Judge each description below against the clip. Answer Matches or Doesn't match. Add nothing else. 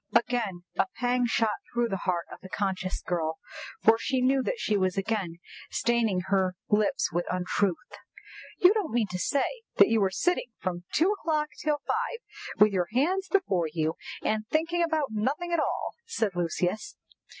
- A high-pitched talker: Matches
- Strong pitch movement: Matches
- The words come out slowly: Doesn't match